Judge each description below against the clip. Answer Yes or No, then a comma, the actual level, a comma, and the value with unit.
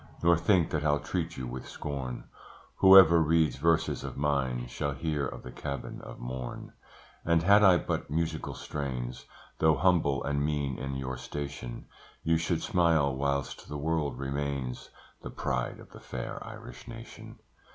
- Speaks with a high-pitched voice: No, very low, 75 Hz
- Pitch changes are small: No, average, 3.7 semitones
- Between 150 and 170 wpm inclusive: Yes, average, 160 wpm